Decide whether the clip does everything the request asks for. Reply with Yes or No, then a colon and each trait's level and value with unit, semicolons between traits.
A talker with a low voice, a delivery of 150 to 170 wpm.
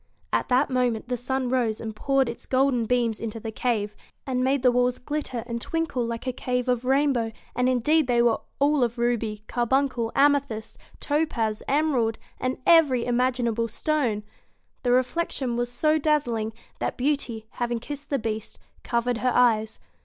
No: high, 245 Hz; average, 165 wpm